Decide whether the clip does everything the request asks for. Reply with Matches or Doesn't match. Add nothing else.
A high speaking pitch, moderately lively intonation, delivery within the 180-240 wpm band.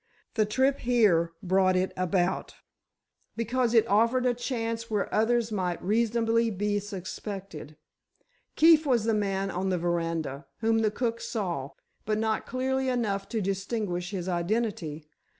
Doesn't match